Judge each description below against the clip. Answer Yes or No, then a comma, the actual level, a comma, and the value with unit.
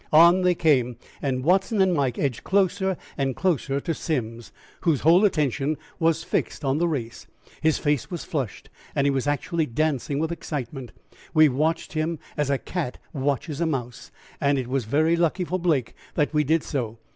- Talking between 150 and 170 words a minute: No, average, 180 wpm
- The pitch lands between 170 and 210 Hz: No, medium, 150 Hz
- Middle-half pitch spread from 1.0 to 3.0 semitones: No, average, 3.8 semitones